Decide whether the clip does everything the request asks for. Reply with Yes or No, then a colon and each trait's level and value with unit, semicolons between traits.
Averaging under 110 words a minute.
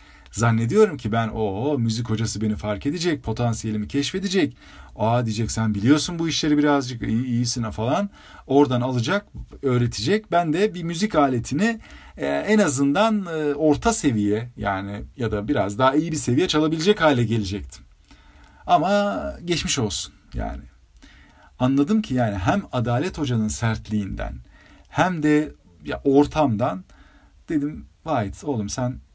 No: average, 125 wpm